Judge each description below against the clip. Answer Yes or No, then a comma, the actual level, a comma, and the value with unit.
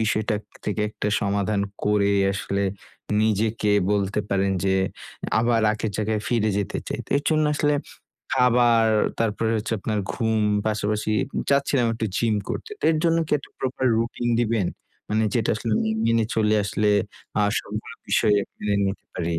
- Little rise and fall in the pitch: Yes, narrow, 2.0 semitones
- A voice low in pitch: Yes, low, 110 Hz